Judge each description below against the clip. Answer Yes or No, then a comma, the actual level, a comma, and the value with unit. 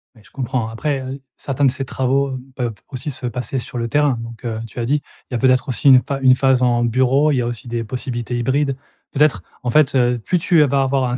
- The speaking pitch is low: Yes, low, 130 Hz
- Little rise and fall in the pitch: Yes, narrow, 2.3 semitones